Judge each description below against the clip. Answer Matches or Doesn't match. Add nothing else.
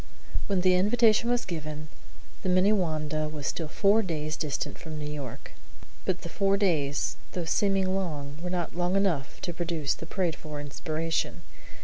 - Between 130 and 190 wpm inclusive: Matches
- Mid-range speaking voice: Matches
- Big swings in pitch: Doesn't match